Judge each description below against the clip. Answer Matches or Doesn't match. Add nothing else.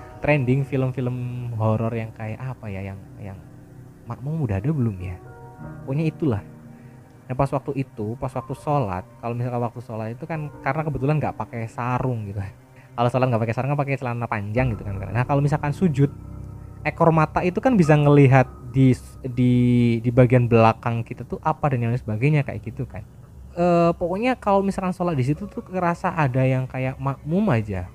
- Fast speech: Matches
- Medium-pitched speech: Doesn't match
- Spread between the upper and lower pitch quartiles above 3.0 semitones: Matches